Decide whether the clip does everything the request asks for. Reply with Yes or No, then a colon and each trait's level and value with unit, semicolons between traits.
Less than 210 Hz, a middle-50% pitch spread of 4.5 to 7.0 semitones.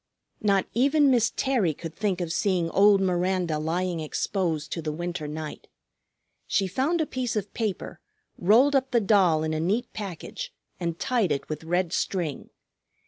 Yes: medium, 185 Hz; average, 5.0 semitones